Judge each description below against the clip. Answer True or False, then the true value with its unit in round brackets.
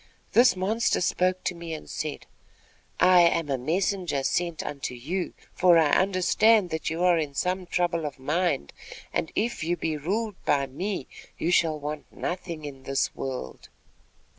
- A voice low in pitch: False (170 Hz)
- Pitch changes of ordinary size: True (3.8 semitones)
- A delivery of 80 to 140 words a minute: False (165 wpm)